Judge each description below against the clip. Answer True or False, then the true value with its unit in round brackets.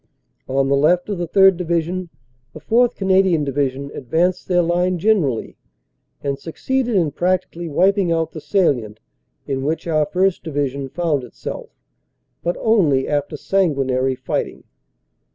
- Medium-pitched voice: True (165 Hz)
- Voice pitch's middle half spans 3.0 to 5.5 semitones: True (4.7 semitones)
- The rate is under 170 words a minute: True (140 wpm)